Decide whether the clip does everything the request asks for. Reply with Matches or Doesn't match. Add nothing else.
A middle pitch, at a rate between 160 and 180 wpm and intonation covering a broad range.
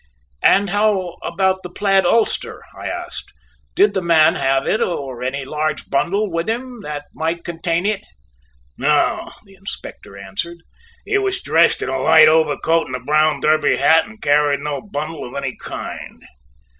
Doesn't match